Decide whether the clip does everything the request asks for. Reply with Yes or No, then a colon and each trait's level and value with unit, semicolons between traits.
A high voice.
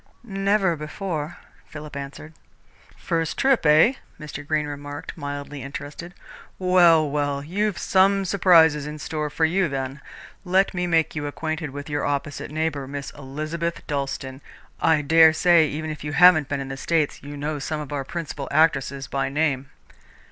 No: medium, 150 Hz